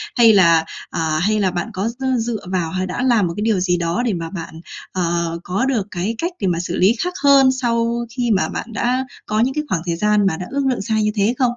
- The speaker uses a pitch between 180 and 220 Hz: Yes, high, 210 Hz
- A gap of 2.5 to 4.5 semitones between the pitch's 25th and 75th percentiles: No, average, 5.2 semitones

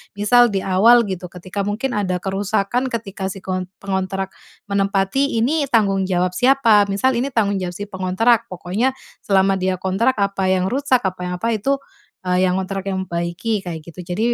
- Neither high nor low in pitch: No, high, 195 Hz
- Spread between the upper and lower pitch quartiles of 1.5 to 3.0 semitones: No, average, 3.5 semitones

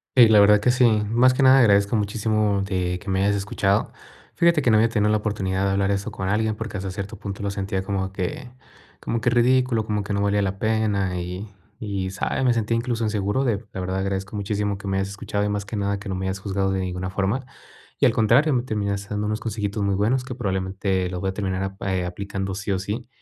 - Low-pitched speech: Yes, low, 100 Hz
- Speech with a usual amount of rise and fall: No, narrow, 2.2 semitones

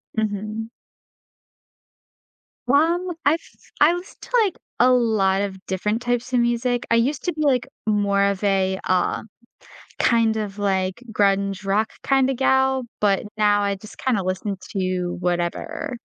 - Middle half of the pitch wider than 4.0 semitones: Yes, average, 4.4 semitones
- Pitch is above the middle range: Yes, high, 215 Hz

